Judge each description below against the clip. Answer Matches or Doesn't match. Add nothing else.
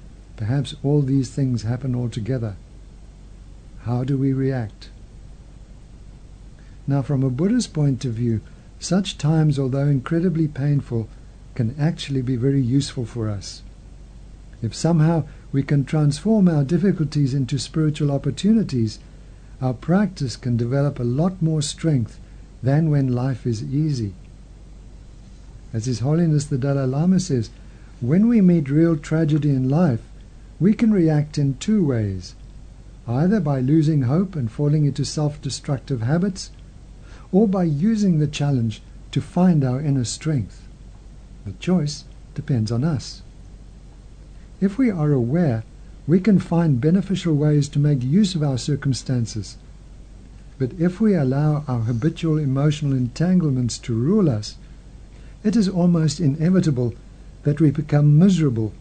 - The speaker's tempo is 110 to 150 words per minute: Matches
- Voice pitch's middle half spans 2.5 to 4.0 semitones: Doesn't match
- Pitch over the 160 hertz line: Doesn't match